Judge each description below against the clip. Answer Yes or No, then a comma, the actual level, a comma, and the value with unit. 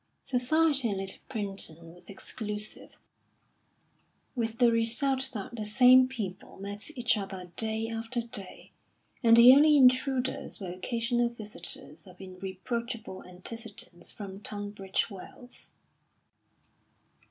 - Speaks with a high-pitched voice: Yes, high, 225 Hz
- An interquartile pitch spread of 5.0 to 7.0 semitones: No, average, 4.1 semitones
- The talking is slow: Yes, slow, 110 wpm